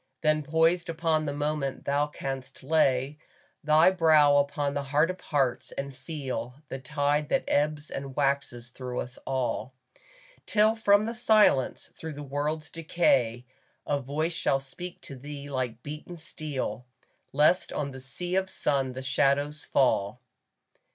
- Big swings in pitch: No, average, 2.7 semitones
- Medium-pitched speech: Yes, medium, 145 Hz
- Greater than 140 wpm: Yes, average, 150 wpm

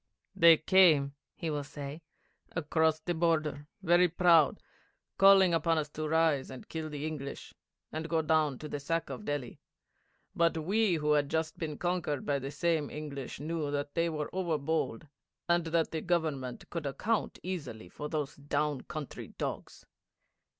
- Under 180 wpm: Yes, average, 165 wpm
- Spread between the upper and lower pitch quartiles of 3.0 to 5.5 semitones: No, narrow, 2.4 semitones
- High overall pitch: No, medium, 155 Hz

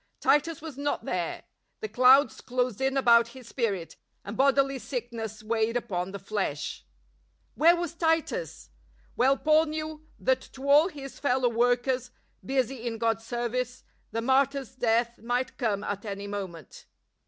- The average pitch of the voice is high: Yes, very high, 250 Hz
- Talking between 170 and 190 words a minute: No, average, 145 wpm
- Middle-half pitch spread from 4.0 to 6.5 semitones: No, average, 3.4 semitones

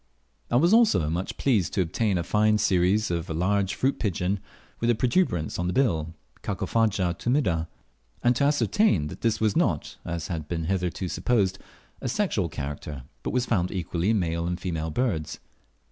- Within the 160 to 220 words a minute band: Yes, average, 175 wpm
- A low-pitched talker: Yes, very low, 95 Hz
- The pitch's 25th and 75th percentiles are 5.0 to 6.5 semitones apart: Yes, wide, 5.5 semitones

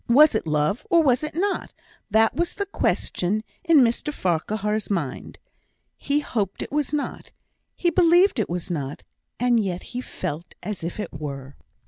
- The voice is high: Yes, high, 220 Hz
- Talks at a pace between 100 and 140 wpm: No, average, 165 wpm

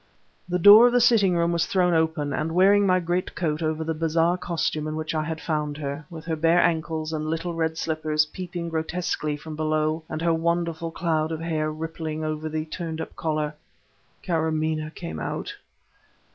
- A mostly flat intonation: Yes, narrow, 1.6 semitones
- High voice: No, medium, 160 Hz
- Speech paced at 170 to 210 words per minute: Yes, average, 185 wpm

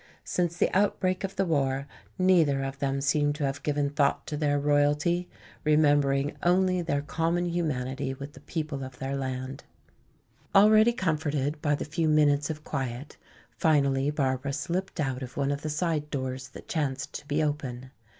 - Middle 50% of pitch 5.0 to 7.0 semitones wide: No, average, 2.8 semitones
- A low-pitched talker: No, medium, 145 Hz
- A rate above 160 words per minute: Yes, average, 170 wpm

